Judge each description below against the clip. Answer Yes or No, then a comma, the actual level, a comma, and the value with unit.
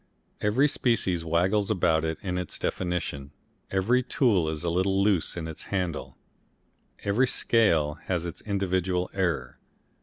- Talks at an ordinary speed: No, slow, 130 wpm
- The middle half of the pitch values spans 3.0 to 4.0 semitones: Yes, average, 3.5 semitones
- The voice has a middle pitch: No, very low, 90 Hz